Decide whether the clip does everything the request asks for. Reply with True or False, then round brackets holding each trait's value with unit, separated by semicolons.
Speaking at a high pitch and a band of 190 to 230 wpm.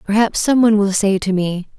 True (205 Hz; 200 wpm)